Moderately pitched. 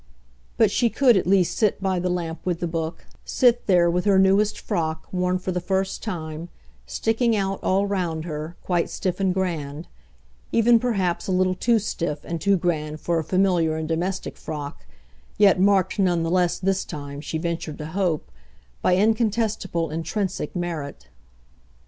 Yes: medium, 180 Hz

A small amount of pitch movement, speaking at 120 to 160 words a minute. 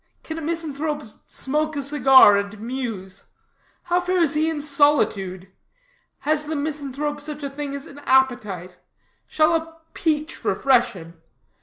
No: average, 3.8 semitones; average, 140 wpm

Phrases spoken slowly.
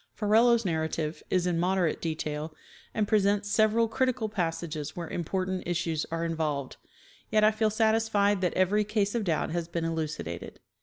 No: average, 155 wpm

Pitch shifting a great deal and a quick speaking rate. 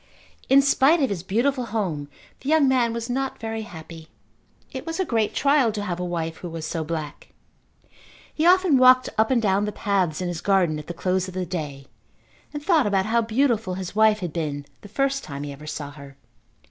Yes: wide, 7.5 semitones; fast, 210 wpm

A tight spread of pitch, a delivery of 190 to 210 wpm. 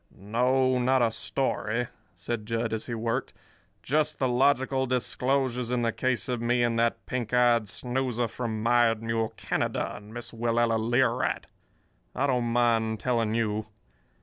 No: narrow, 1.8 semitones; average, 155 wpm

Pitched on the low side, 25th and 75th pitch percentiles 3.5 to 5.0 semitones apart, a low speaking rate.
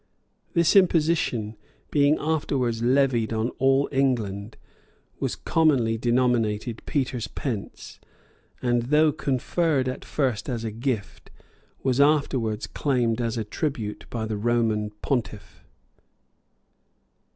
Yes: low, 125 Hz; average, 4.0 semitones; slow, 105 wpm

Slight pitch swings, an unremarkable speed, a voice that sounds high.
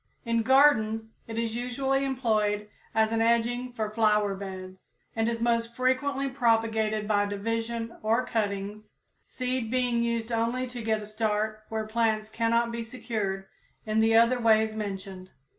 Yes: narrow, 1.7 semitones; average, 150 wpm; high, 225 Hz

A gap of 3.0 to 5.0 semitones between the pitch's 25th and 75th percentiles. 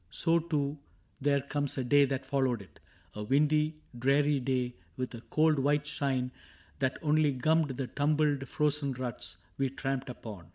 No: narrow, 2.6 semitones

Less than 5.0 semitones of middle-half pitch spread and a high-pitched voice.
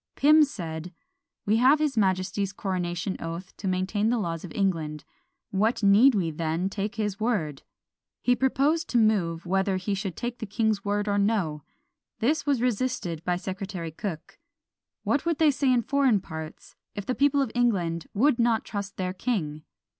No: average, 5.3 semitones; high, 200 Hz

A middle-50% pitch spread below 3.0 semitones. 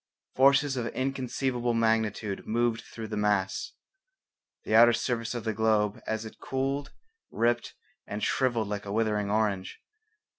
Yes: narrow, 2.6 semitones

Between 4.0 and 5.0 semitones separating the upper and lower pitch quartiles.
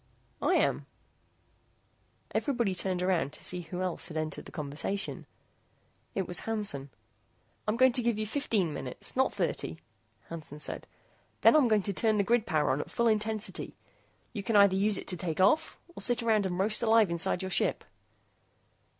Yes: average, 4.4 semitones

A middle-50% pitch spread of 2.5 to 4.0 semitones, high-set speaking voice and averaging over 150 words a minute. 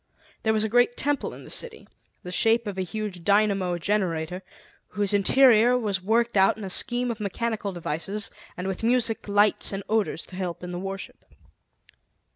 Yes: average, 3.2 semitones; high, 205 Hz; average, 180 wpm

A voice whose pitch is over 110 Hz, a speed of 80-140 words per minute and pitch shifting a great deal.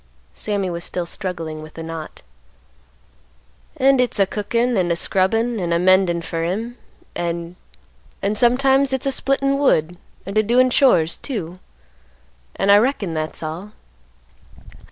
Yes: high, 190 Hz; slow, 135 wpm; wide, 6.2 semitones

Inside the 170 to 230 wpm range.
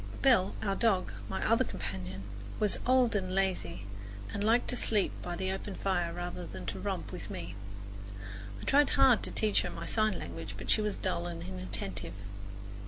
Yes: average, 180 wpm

